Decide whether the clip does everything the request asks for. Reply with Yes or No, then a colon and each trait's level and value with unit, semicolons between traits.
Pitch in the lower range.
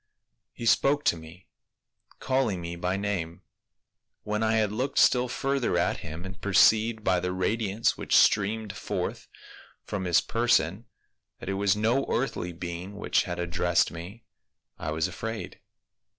Yes: low, 100 Hz